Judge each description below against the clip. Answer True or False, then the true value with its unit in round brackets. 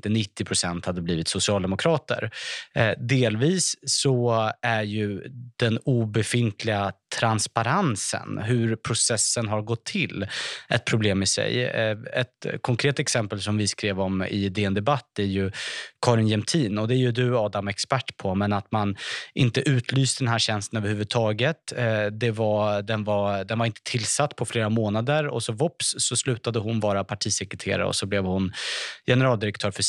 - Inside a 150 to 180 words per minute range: True (165 wpm)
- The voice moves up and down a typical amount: True (3.3 semitones)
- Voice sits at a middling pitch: False (110 Hz)